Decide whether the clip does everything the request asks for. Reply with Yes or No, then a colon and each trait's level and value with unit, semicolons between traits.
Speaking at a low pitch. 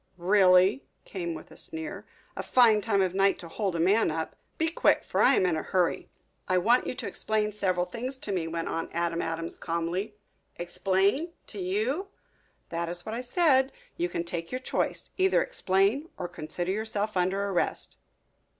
No: high, 190 Hz